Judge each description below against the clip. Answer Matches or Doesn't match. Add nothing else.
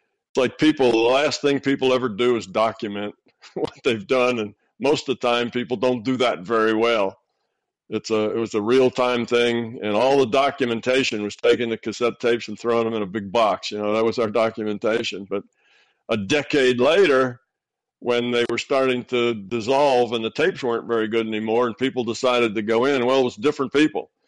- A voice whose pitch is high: Doesn't match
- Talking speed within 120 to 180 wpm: Doesn't match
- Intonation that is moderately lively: Doesn't match